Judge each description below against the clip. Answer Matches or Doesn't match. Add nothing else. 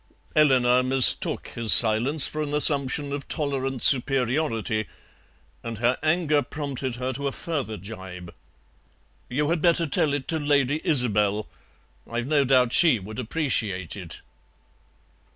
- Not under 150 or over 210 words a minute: Doesn't match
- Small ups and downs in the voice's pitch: Doesn't match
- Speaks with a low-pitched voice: Matches